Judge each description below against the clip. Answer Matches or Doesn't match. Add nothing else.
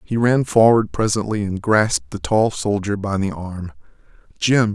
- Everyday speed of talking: Matches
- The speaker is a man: Matches